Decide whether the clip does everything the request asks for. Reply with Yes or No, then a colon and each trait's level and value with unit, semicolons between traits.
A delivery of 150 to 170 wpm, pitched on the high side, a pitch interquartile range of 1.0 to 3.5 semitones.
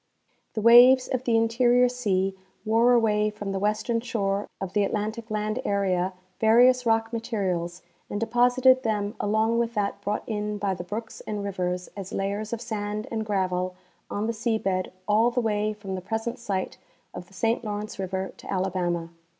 No: average, 180 wpm; high, 210 Hz; average, 2.9 semitones